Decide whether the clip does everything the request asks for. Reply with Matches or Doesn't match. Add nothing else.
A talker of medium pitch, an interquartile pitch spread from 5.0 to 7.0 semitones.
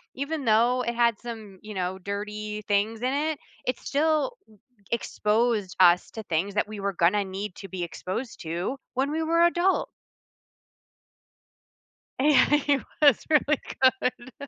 Doesn't match